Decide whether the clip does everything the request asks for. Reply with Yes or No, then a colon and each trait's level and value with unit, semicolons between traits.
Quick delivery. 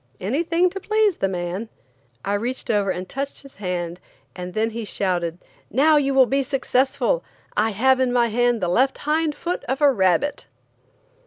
No: average, 175 wpm